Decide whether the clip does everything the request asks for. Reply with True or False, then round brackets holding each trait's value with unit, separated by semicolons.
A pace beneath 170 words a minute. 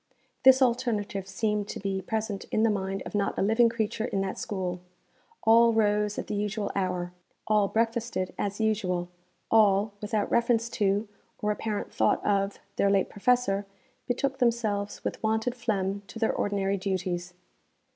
True (155 wpm)